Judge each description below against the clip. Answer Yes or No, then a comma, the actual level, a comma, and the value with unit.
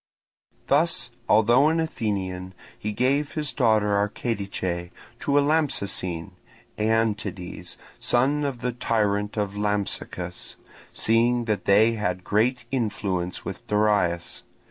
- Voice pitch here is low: Yes, low, 105 Hz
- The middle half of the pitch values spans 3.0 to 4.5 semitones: Yes, average, 3.5 semitones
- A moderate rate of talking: No, slow, 110 wpm